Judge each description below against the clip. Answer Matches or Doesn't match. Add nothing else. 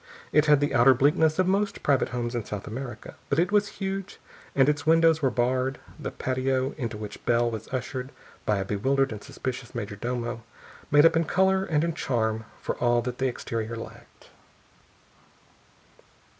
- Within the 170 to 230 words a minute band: Matches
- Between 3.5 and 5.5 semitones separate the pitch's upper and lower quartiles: Matches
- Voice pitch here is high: Doesn't match